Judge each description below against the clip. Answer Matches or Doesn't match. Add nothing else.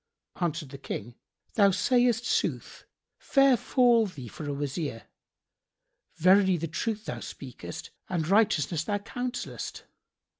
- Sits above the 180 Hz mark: Matches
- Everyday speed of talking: Doesn't match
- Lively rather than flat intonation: Matches